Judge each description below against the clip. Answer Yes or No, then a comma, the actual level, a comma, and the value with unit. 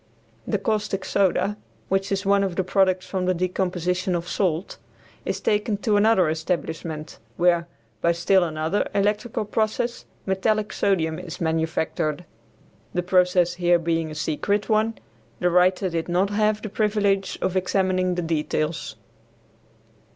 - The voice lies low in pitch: No, medium, 185 Hz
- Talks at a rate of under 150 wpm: Yes, average, 140 wpm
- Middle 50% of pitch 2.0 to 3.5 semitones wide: Yes, average, 3.0 semitones